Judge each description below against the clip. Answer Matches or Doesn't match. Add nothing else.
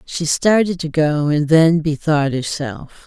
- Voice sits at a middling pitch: Matches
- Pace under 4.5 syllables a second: Matches